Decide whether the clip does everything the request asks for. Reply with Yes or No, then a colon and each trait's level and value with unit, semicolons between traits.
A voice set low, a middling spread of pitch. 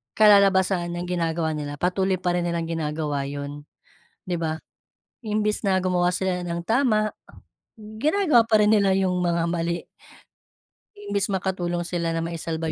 No: medium, 180 Hz; average, 3.2 semitones